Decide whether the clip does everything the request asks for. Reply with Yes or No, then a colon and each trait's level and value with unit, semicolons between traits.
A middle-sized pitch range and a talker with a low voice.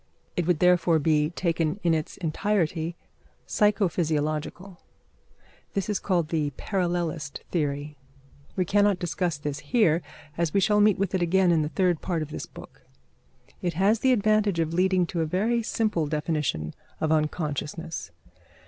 No: average, 3.6 semitones; medium, 170 Hz